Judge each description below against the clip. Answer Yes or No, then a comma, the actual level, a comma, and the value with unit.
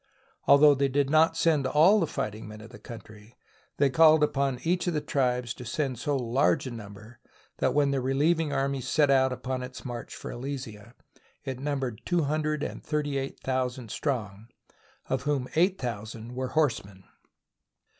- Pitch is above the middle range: No, low, 135 Hz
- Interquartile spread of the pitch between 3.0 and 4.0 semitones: Yes, average, 3.5 semitones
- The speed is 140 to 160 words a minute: No, average, 175 wpm